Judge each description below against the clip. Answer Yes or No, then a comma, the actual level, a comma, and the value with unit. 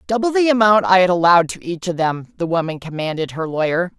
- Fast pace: Yes, fast, 225 wpm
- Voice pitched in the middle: Yes, medium, 180 Hz